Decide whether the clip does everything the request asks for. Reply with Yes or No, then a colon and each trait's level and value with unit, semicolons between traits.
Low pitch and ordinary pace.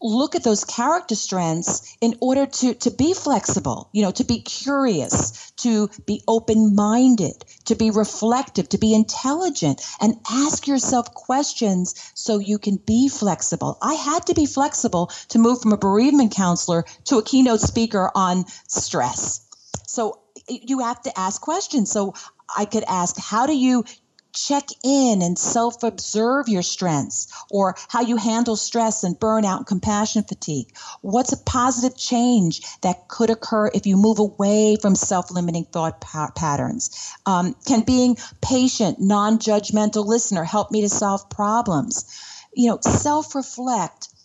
No: high, 220 Hz; average, 155 wpm